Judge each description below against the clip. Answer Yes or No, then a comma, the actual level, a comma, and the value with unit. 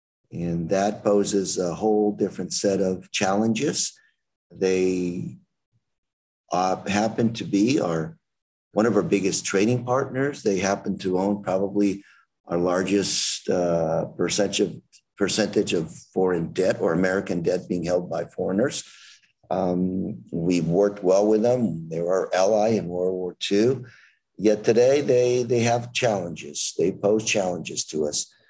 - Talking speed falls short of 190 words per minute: Yes, average, 140 wpm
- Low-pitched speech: Yes, very low, 95 Hz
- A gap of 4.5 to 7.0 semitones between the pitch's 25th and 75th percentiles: No, average, 2.8 semitones